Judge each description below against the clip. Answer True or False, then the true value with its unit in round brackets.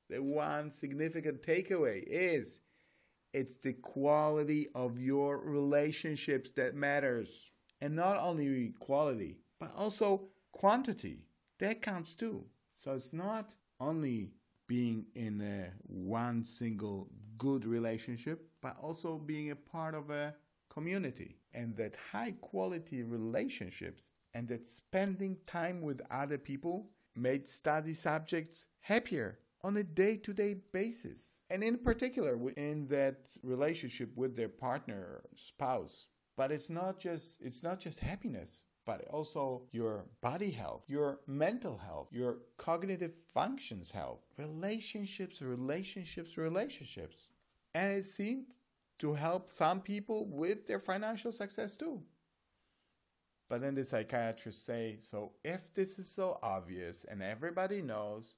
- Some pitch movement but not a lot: False (7.4 semitones)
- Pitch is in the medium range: True (150 Hz)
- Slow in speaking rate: True (125 wpm)